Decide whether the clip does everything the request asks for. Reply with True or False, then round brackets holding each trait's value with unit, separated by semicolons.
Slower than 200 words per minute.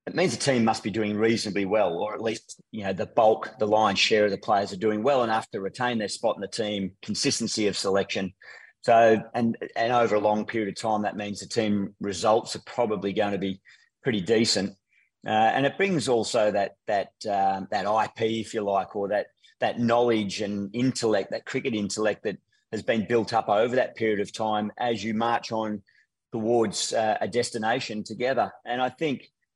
False (205 wpm)